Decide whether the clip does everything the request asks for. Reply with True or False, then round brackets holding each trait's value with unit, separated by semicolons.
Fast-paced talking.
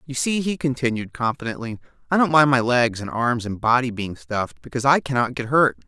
True (215 wpm)